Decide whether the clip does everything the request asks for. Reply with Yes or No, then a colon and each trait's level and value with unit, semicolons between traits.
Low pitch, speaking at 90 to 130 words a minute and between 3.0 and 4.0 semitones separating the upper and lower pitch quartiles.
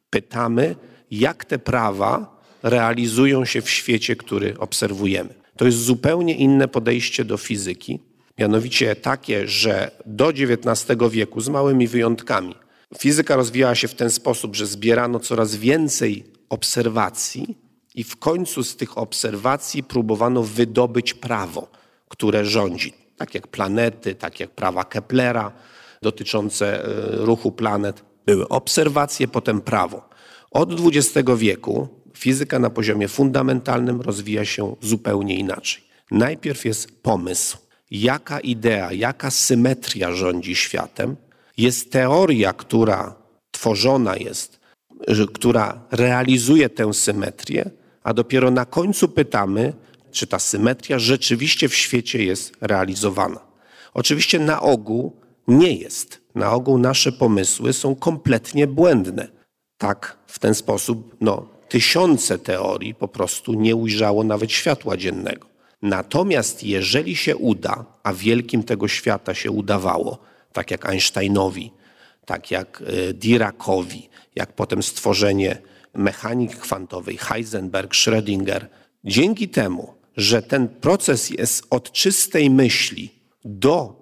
Yes: low, 115 Hz; average, 115 wpm; average, 3.7 semitones